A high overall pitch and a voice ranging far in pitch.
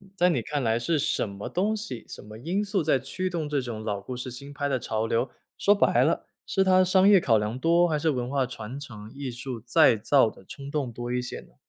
No: low, 135 Hz; wide, 6.1 semitones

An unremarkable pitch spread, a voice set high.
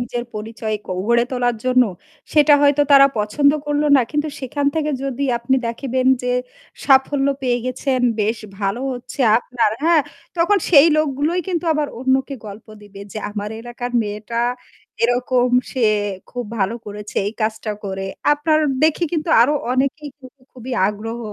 Yes: average, 4.1 semitones; very high, 255 Hz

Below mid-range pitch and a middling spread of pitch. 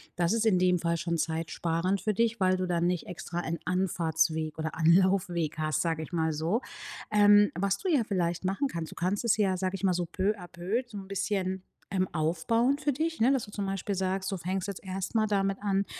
No: medium, 185 Hz; average, 3.2 semitones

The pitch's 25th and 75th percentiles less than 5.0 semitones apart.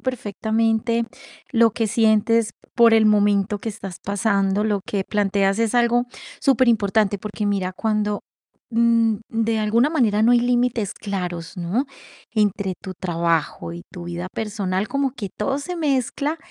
Yes: average, 2.8 semitones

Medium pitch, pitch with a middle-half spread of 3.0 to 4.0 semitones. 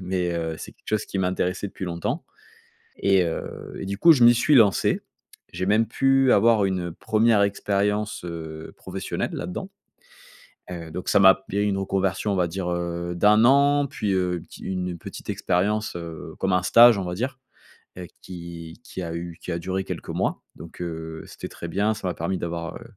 No: very low, 95 Hz; average, 3.3 semitones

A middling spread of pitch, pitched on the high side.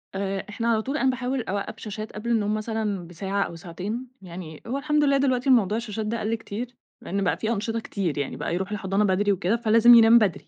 Yes: average, 3.2 semitones; high, 215 Hz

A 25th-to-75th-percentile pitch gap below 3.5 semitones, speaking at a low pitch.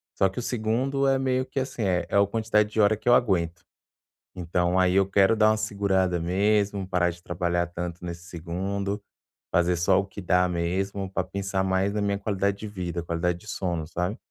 Yes: average, 2.9 semitones; very low, 95 Hz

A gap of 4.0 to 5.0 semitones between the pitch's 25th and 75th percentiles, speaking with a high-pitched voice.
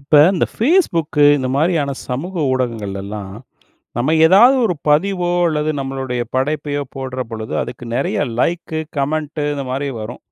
No: average, 4.6 semitones; medium, 140 Hz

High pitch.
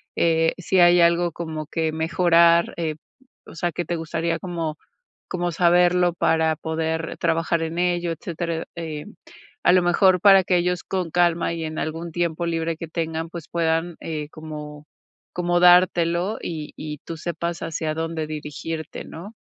No: medium, 165 Hz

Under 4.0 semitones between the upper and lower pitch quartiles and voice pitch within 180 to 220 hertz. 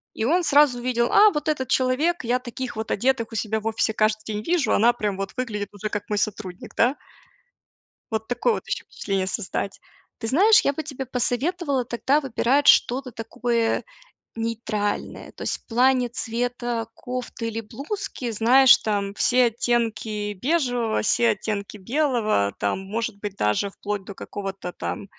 No: average, 3.4 semitones; high, 230 Hz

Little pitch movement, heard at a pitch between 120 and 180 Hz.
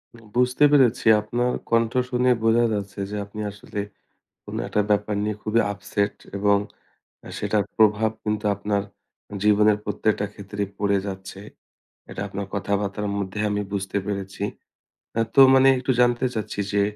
No: narrow, 1.9 semitones; low, 105 Hz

